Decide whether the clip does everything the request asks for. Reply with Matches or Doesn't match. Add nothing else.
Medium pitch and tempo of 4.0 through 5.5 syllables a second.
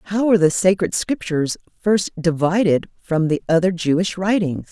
Matches